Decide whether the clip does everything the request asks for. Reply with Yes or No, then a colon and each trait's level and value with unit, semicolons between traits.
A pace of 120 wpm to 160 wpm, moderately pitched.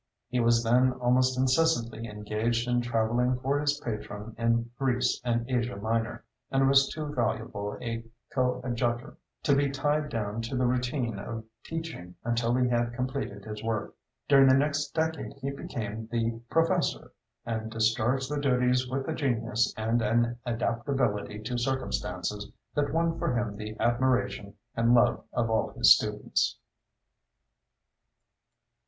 No: average, 145 wpm; low, 120 Hz